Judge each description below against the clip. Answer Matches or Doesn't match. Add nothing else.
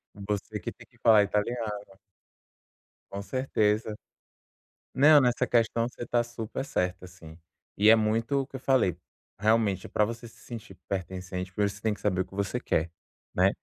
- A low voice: Matches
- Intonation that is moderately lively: Matches